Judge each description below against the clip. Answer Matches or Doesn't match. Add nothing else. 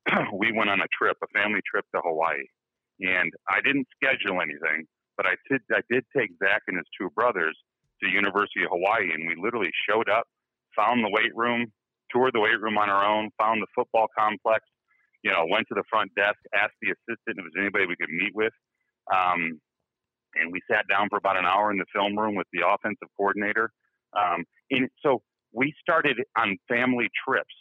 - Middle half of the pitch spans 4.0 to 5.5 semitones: Doesn't match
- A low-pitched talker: Matches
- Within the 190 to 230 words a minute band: Matches